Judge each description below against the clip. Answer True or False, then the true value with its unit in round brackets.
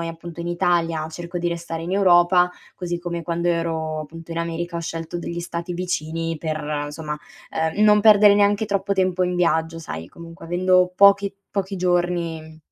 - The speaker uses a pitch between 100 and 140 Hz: False (170 Hz)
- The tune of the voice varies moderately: False (1.7 semitones)